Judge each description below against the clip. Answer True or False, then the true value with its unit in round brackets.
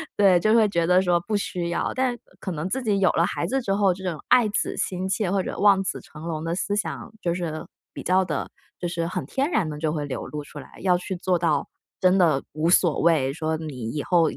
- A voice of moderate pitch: True (180 Hz)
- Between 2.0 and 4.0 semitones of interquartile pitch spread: True (3.6 semitones)